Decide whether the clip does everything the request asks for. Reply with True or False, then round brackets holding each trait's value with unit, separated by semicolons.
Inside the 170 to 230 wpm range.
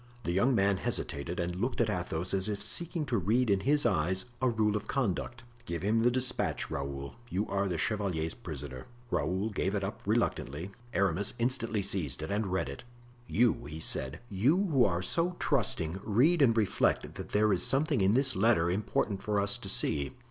True (190 wpm)